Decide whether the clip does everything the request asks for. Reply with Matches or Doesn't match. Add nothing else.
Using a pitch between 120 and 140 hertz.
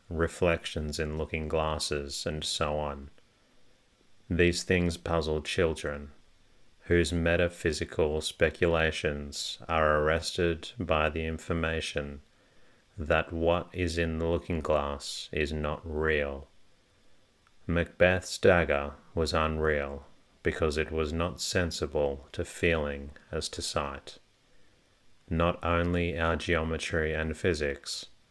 Doesn't match